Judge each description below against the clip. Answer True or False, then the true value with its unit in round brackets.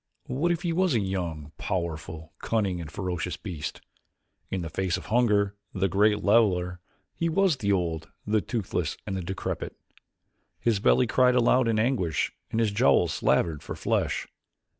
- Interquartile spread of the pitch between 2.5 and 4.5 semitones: False (4.9 semitones)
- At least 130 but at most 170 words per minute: True (165 wpm)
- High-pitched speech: False (100 Hz)